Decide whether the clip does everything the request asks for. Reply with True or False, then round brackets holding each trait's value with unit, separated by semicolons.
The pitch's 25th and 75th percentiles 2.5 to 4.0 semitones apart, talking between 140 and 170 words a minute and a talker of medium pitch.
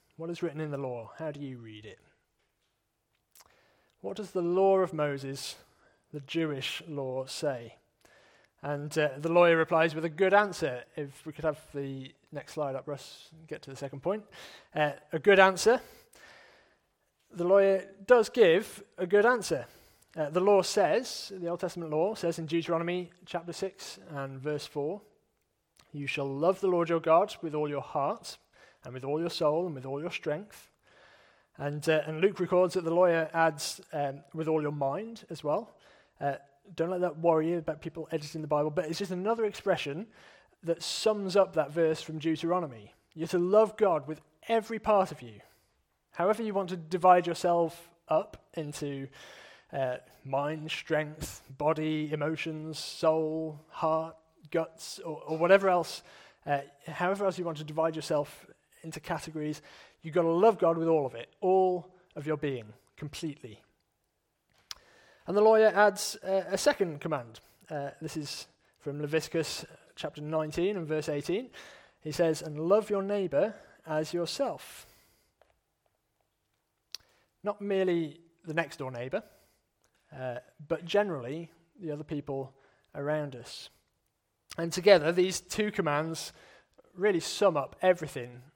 True (3.7 semitones; 160 wpm; 160 Hz)